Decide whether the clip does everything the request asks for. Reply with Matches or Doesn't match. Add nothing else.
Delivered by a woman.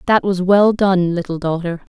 Matches